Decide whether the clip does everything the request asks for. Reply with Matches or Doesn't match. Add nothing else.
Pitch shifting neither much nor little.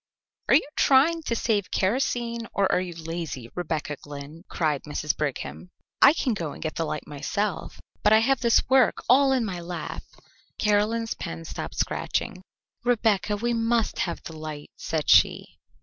Doesn't match